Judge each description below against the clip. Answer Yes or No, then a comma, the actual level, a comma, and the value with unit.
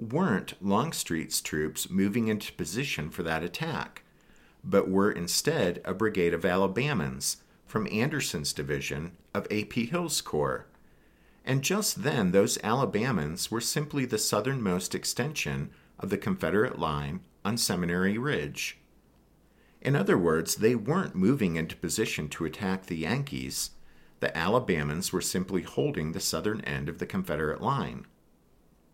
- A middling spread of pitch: No, wide, 6.3 semitones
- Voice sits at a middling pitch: No, very low, 95 Hz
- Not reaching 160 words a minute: Yes, slow, 135 wpm